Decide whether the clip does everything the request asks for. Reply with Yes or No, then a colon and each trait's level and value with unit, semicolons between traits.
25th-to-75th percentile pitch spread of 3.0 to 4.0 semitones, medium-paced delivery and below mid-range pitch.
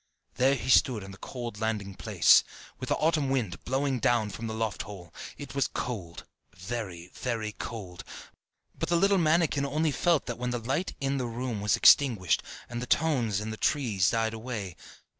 No: average, 4.7 semitones; average, 180 wpm; low, 120 Hz